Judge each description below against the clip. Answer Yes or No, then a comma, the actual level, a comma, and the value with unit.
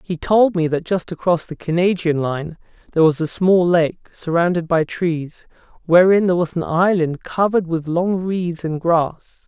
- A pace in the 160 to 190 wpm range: Yes, average, 175 wpm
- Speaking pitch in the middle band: Yes, medium, 170 Hz